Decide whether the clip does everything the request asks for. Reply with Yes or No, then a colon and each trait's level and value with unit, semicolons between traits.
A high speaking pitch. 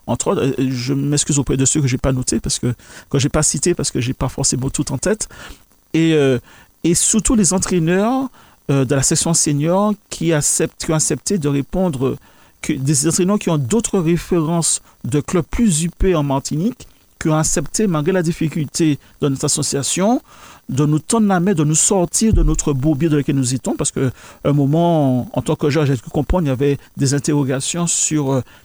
No: medium, 155 Hz